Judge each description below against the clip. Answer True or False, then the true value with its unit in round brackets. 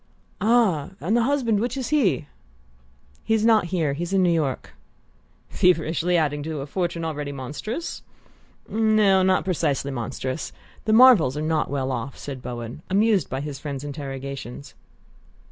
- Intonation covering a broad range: True (6.7 semitones)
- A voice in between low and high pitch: True (160 Hz)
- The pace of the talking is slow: False (145 wpm)